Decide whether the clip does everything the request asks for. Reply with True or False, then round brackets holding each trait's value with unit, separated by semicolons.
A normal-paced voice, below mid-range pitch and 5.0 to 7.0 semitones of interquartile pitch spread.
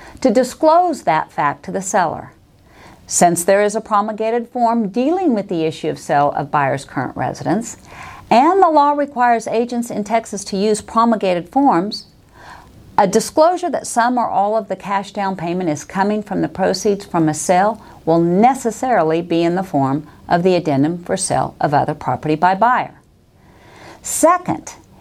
False (170 wpm; 210 Hz; 5.5 semitones)